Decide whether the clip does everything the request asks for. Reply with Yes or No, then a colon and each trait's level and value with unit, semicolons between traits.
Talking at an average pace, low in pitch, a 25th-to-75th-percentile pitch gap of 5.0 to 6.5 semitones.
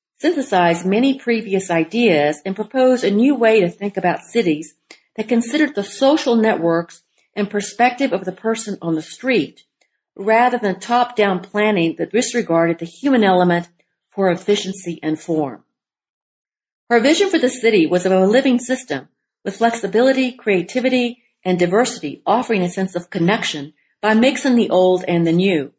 No: average, 155 wpm; high, 205 Hz; wide, 5.4 semitones